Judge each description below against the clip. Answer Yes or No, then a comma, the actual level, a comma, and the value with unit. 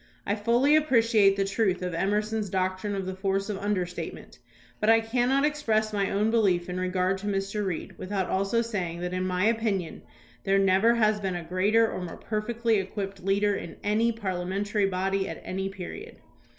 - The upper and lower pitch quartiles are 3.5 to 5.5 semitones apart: No, average, 2.8 semitones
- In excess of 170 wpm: Yes, average, 180 wpm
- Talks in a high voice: Yes, high, 195 Hz